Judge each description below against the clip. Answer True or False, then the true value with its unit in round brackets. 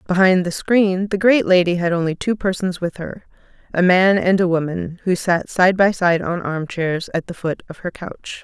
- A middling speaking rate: False (220 wpm)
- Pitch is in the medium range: True (180 Hz)